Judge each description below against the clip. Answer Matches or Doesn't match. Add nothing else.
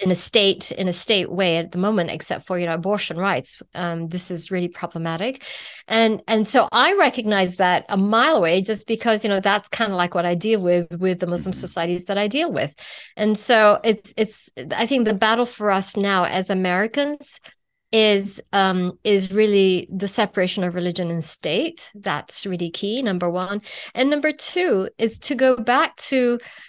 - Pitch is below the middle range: Doesn't match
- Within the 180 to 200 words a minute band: Matches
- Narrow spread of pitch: Doesn't match